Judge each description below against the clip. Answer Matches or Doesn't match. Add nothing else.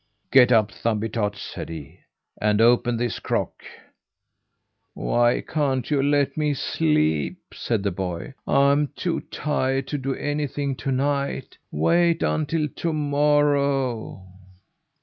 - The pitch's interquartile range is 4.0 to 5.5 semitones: Matches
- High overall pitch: Doesn't match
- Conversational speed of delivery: Doesn't match